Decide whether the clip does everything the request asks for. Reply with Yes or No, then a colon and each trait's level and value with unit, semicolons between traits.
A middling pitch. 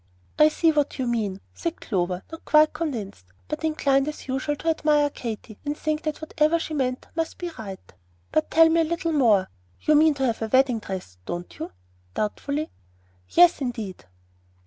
No: very high, 290 Hz